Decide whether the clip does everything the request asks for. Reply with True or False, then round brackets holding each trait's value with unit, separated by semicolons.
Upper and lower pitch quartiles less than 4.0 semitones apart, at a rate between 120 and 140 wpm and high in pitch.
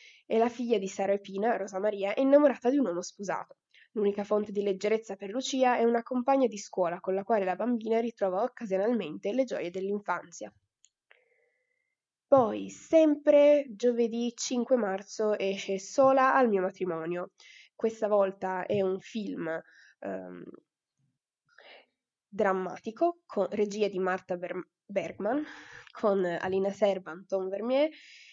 False (4.5 semitones; 135 wpm; 205 Hz)